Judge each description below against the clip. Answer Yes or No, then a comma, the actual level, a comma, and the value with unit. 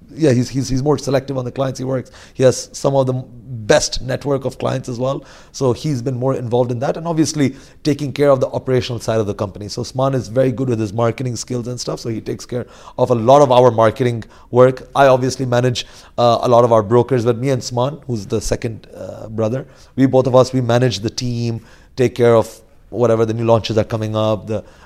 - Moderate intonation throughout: No, narrow, 2.3 semitones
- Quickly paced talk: Yes, fast, 240 wpm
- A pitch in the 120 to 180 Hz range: Yes, low, 125 Hz